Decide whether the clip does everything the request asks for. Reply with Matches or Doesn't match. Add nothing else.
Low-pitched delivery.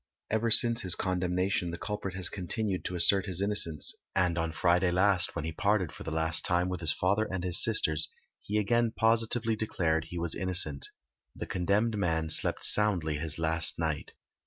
Matches